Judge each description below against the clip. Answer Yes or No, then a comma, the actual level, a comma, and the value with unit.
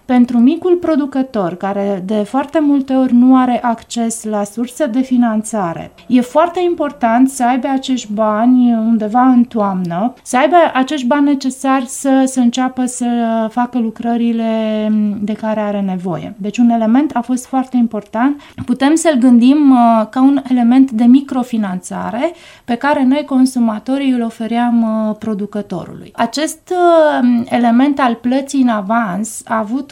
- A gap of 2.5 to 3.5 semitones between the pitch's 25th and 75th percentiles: Yes, average, 3.1 semitones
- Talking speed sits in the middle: Yes, average, 140 wpm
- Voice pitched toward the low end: No, high, 245 Hz